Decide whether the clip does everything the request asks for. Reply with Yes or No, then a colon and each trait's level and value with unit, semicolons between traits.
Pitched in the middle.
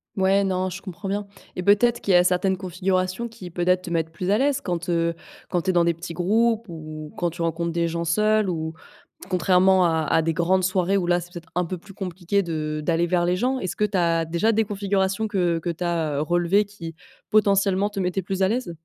Yes: medium, 180 Hz